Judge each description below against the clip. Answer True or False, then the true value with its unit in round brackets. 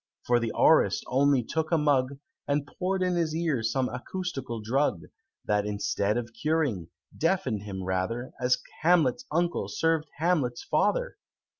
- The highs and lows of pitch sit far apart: True (6.0 semitones)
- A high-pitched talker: False (135 Hz)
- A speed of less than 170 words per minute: True (145 wpm)